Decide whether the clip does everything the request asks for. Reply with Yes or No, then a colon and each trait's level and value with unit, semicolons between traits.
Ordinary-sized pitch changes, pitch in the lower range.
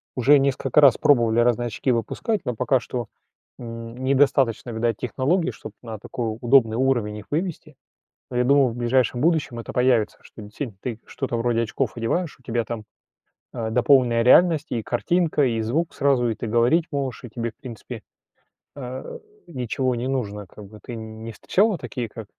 Yes: average, 3.0 semitones; low, 120 Hz